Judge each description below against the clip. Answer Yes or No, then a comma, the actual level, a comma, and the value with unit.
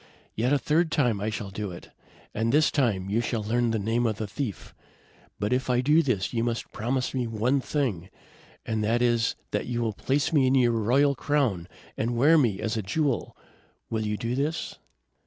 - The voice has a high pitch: No, low, 120 Hz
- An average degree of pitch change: Yes, average, 3.7 semitones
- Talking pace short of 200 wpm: No, fast, 205 wpm